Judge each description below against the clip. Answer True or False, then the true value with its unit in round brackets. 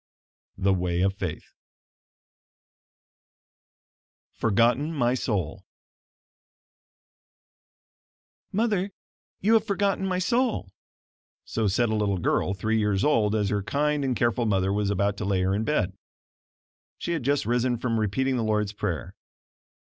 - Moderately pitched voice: False (110 Hz)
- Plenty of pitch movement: True (6.2 semitones)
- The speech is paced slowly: True (130 wpm)